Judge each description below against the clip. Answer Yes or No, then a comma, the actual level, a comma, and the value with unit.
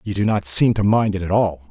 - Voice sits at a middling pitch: No, low, 100 Hz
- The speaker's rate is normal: No, fast, 315 wpm